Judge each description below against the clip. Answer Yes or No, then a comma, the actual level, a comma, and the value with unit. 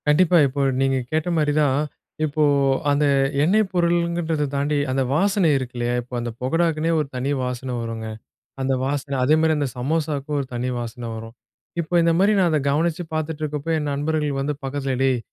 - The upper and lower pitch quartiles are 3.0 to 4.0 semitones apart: Yes, average, 3.3 semitones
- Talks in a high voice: No, medium, 145 Hz